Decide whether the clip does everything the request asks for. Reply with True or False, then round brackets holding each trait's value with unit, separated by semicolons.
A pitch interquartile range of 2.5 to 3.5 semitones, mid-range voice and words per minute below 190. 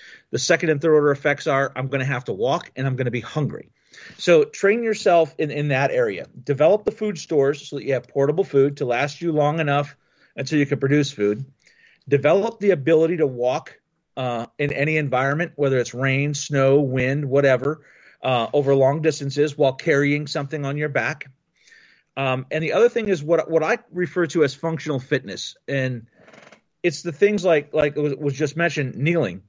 False (2.9 semitones; 145 Hz; 200 wpm)